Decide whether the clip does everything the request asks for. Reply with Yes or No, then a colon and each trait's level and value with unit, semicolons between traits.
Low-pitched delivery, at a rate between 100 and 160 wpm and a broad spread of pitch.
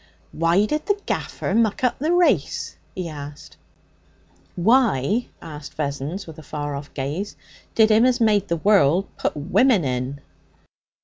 No: medium, 180 Hz; average, 145 wpm; wide, 7.3 semitones